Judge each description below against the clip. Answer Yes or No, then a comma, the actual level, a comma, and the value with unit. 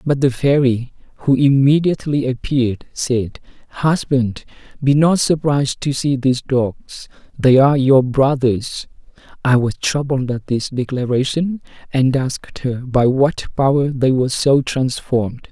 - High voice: No, low, 130 Hz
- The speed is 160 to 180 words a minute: No, slow, 135 wpm